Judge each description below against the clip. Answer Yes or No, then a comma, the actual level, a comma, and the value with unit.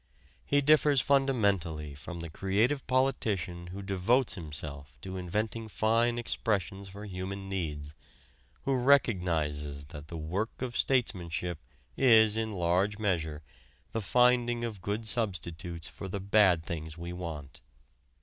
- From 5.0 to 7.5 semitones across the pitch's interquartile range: Yes, wide, 5.4 semitones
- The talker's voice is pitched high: No, very low, 95 Hz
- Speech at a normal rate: No, slow, 130 wpm